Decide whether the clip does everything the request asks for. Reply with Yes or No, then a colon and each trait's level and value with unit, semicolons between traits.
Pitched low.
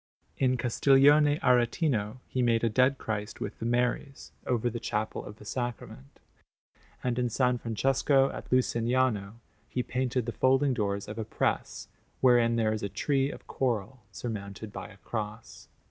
Yes: low, 120 Hz